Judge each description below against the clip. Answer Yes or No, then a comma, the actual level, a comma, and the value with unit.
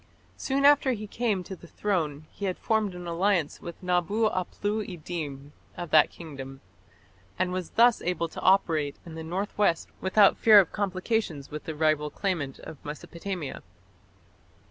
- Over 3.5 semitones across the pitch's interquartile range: Yes, average, 4.5 semitones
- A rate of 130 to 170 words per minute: Yes, average, 160 wpm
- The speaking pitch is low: No, medium, 180 Hz